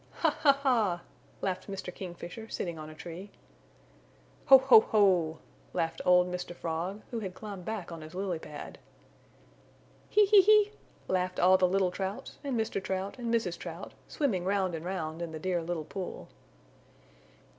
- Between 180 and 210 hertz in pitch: Yes, medium, 185 Hz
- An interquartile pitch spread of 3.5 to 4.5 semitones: Yes, average, 3.8 semitones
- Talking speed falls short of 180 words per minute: Yes, average, 165 wpm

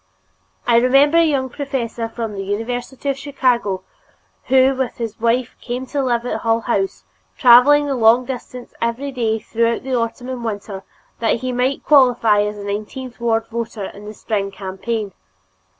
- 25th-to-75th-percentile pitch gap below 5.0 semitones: Yes, average, 2.7 semitones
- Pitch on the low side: No, high, 235 Hz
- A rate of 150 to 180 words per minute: Yes, average, 165 wpm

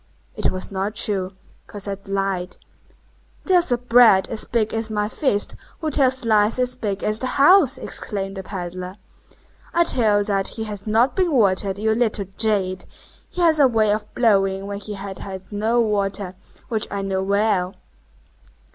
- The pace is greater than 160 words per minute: Yes, average, 170 wpm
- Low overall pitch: No, high, 210 Hz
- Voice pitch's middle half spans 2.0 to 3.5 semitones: Yes, average, 3.2 semitones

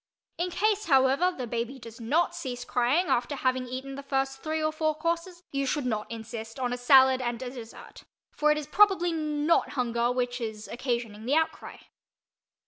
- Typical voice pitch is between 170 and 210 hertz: No, very high, 265 Hz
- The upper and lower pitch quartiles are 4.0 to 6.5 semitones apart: Yes, average, 4.3 semitones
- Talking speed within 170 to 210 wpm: Yes, average, 185 wpm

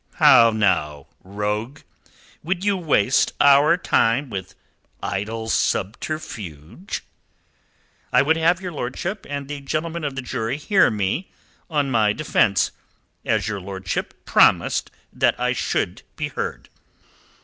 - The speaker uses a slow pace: Yes, slow, 125 wpm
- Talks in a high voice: No, low, 130 Hz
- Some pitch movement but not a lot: No, wide, 6.9 semitones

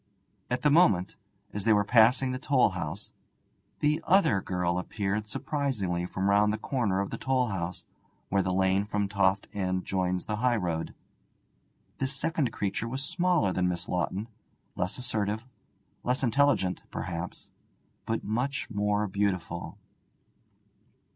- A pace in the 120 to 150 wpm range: Yes, average, 140 wpm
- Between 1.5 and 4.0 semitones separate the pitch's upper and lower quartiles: No, average, 5.2 semitones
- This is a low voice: Yes, low, 105 Hz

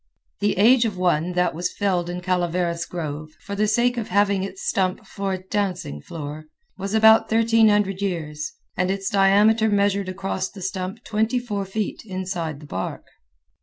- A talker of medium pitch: No, high, 195 Hz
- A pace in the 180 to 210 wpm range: No, average, 165 wpm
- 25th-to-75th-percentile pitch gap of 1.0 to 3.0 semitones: Yes, narrow, 2.6 semitones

